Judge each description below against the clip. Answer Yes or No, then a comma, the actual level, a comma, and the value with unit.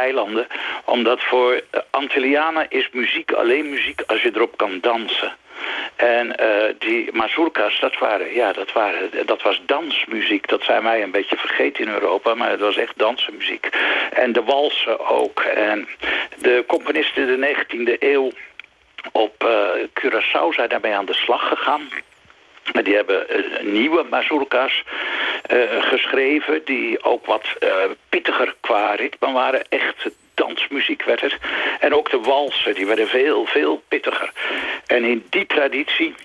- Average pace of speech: Yes, average, 145 wpm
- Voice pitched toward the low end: No, very high, 390 Hz